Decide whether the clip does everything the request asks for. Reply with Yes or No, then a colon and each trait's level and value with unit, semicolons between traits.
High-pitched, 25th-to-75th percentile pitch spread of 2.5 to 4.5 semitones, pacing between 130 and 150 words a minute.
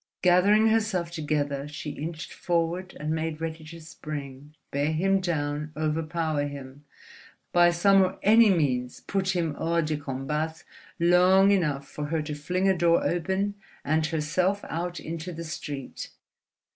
No: medium, 165 Hz; average, 3.2 semitones; average, 145 wpm